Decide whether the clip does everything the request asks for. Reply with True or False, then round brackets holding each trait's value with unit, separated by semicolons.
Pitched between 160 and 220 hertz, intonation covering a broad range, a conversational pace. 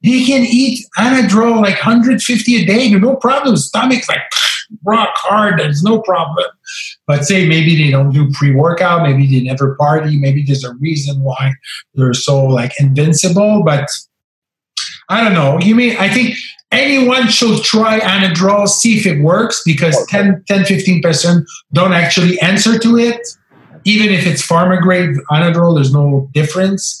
True (185 Hz; 7.0 semitones; 160 wpm)